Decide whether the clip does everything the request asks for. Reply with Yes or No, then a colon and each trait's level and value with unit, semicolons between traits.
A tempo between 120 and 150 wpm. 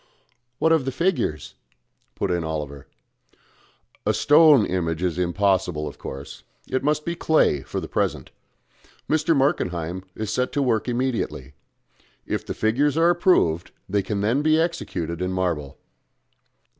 Yes: average, 145 wpm